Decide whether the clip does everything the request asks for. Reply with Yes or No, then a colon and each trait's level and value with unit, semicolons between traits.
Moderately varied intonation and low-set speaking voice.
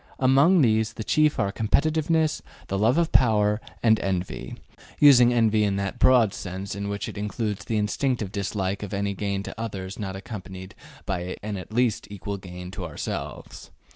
Yes: average, 3.4 semitones; low, 105 Hz